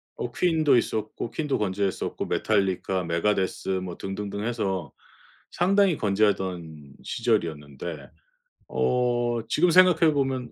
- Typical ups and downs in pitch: No, wide, 6.1 semitones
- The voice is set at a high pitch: No, low, 105 Hz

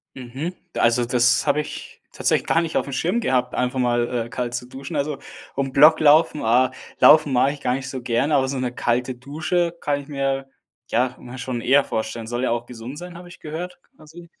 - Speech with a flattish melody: No, average, 3.5 semitones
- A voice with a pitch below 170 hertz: Yes, low, 135 Hz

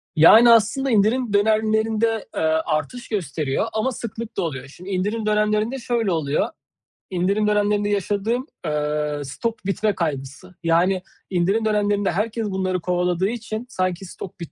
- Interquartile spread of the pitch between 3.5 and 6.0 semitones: Yes, average, 4.0 semitones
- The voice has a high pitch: Yes, high, 205 Hz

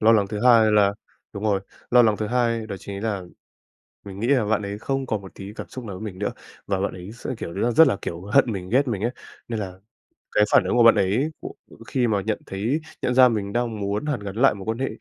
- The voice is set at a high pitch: No, low, 110 Hz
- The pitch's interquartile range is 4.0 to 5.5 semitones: No, average, 3.3 semitones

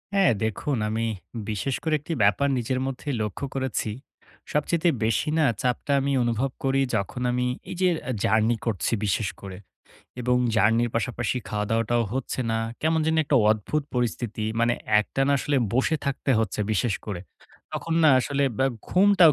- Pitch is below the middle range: Yes, low, 125 Hz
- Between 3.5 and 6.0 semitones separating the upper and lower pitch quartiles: Yes, average, 4.1 semitones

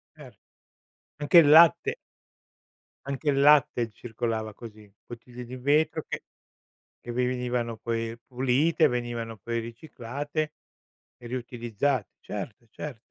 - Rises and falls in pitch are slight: No, average, 3.5 semitones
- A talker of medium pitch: No, low, 125 Hz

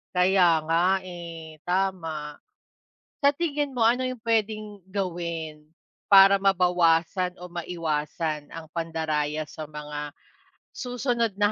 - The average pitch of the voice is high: No, medium, 175 Hz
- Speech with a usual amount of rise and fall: Yes, average, 3.8 semitones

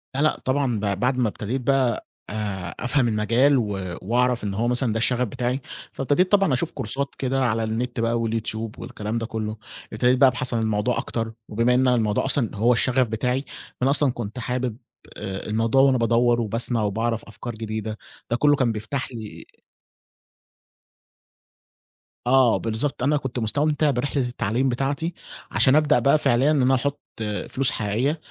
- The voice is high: No, low, 120 Hz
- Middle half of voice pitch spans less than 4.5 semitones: Yes, average, 3.1 semitones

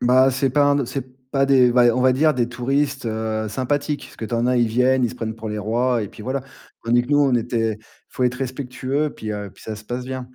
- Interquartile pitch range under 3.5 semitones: Yes, narrow, 2.6 semitones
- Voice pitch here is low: Yes, low, 125 Hz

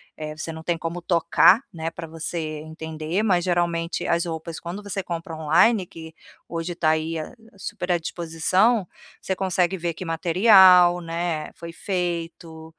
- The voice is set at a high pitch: No, medium, 170 Hz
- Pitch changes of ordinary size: No, narrow, 1.8 semitones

